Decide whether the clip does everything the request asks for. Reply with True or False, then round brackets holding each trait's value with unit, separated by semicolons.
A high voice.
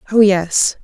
True (195 Hz)